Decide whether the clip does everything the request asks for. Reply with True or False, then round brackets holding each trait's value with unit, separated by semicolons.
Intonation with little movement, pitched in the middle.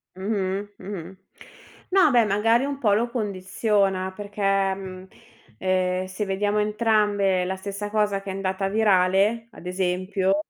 False (1.9 semitones; 195 Hz)